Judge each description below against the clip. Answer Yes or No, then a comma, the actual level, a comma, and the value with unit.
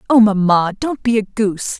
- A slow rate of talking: No, average, 200 wpm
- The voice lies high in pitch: Yes, high, 210 Hz